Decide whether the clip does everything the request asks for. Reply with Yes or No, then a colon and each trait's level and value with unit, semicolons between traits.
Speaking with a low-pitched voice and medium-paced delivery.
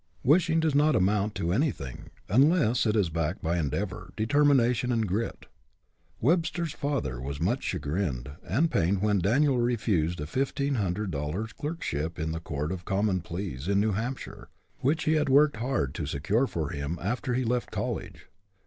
Yes: low, 105 Hz; average, 165 wpm